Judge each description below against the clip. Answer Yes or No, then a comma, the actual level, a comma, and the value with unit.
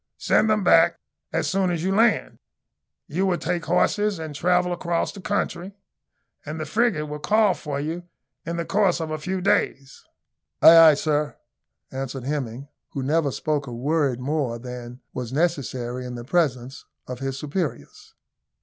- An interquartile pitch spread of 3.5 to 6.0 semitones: Yes, average, 4.7 semitones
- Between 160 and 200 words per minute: Yes, average, 165 wpm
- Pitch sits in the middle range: Yes, medium, 155 Hz